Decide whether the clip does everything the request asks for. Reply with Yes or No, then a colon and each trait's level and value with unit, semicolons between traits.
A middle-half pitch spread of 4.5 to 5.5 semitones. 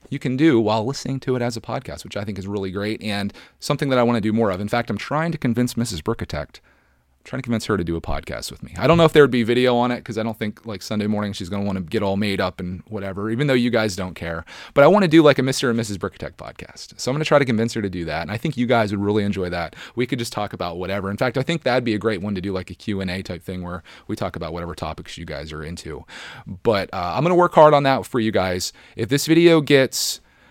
Yes: average, 5.1 semitones